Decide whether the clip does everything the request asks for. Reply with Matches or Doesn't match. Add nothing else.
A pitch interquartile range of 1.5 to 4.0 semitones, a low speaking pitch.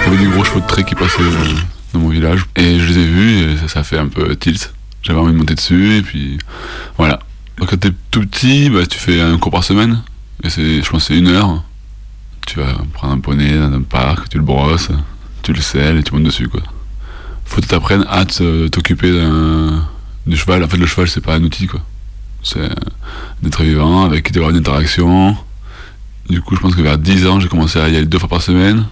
Matches